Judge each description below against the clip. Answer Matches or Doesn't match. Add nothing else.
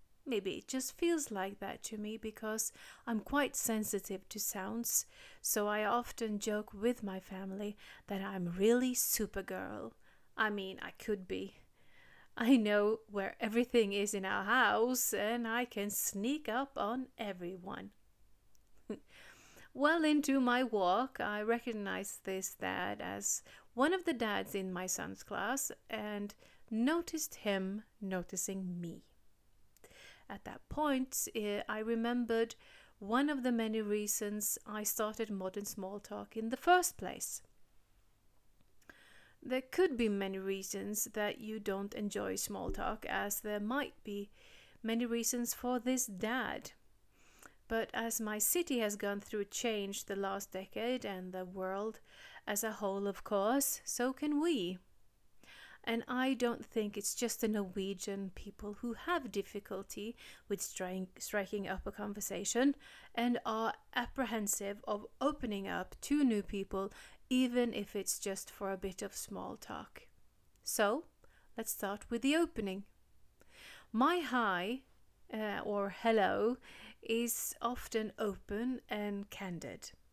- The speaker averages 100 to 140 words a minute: Matches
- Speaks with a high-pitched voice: Matches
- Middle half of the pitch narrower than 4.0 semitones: Matches